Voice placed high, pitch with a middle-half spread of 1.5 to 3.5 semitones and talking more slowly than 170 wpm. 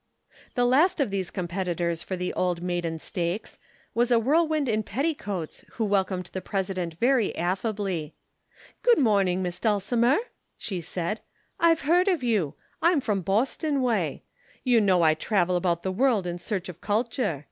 No: high, 200 Hz; wide, 5.6 semitones; average, 160 wpm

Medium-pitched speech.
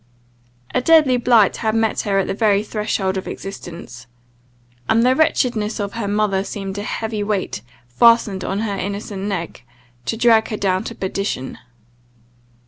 No: high, 205 Hz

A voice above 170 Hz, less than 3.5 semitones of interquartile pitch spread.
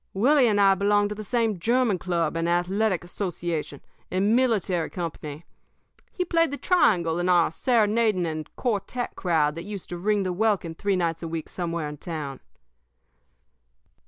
No: medium, 185 Hz; average, 4.3 semitones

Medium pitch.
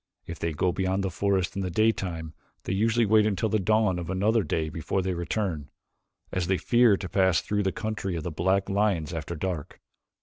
No: very low, 95 Hz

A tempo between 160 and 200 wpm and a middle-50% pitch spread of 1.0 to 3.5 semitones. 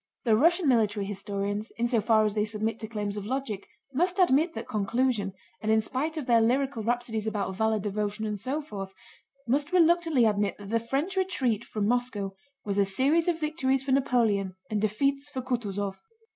No: average, 185 wpm; average, 4.8 semitones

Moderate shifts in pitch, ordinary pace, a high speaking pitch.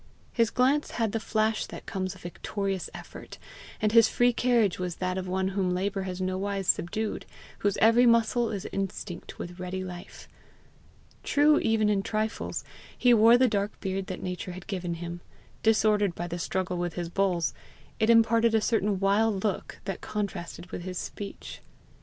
Yes: average, 3.3 semitones; average, 170 wpm; high, 195 Hz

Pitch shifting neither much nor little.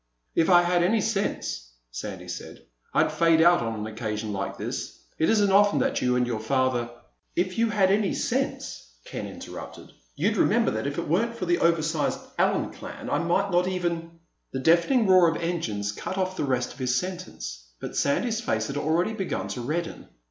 No: wide, 7.3 semitones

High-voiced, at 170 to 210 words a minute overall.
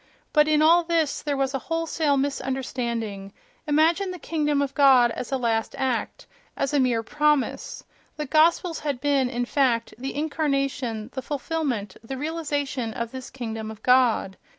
No: very high, 270 Hz; average, 160 wpm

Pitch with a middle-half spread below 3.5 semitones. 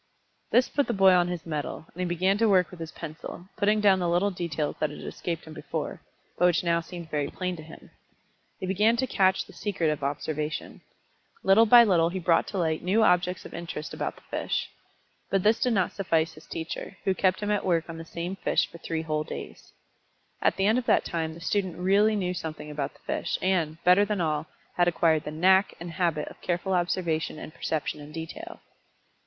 Yes: average, 3.1 semitones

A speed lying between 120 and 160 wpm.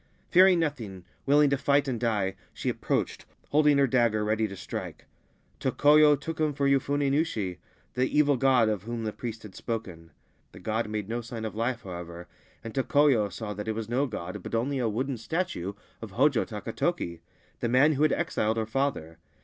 No: average, 190 wpm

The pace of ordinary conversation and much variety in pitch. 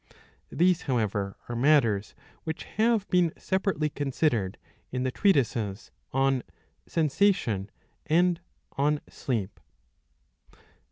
No: slow, 95 wpm; wide, 6.8 semitones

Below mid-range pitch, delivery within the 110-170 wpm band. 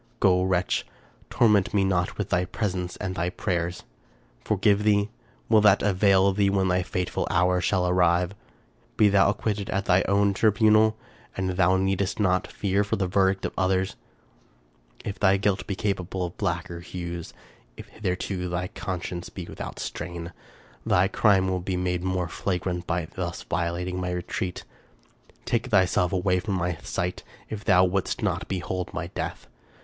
Yes: very low, 95 Hz; average, 165 wpm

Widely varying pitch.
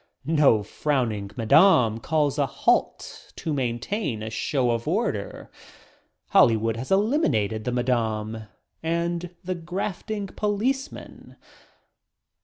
Yes: wide, 8.0 semitones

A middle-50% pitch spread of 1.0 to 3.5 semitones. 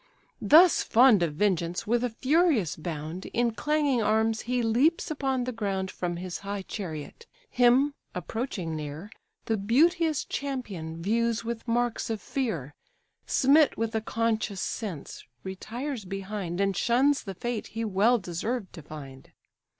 No: average, 5.1 semitones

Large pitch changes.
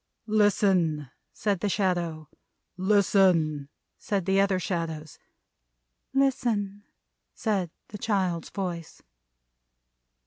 No: average, 3.4 semitones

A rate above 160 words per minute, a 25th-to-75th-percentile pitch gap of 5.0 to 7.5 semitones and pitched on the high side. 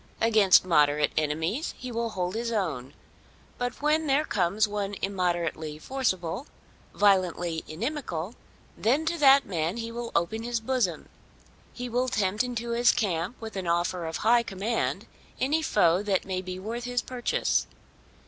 No: average, 150 wpm; wide, 5.5 semitones; high, 210 Hz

